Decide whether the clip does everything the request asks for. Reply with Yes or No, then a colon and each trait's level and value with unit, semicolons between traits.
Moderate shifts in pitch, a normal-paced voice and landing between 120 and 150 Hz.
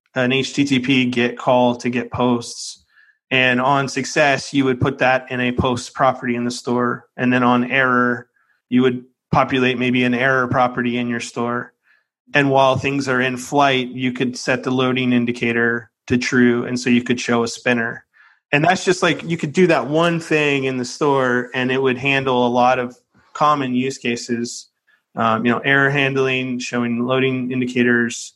No: narrow, 1.5 semitones; average, 185 wpm; low, 125 Hz